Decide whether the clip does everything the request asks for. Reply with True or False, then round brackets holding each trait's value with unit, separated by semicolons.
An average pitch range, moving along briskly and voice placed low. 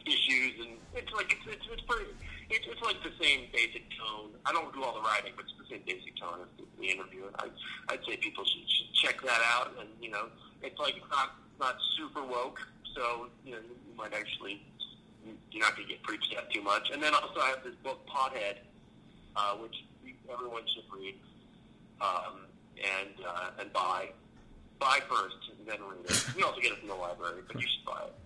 True (4.3 semitones; 215 wpm; 115 Hz)